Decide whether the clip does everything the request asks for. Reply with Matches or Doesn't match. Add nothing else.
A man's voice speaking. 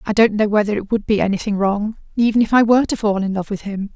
Doesn't match